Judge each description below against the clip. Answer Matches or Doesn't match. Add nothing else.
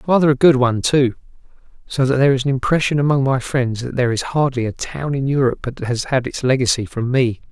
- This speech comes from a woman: Doesn't match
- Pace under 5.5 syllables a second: Doesn't match